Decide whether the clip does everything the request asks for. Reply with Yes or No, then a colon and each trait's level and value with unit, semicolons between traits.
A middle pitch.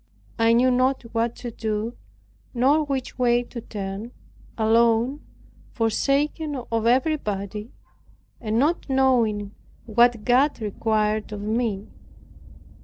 No: high, 235 Hz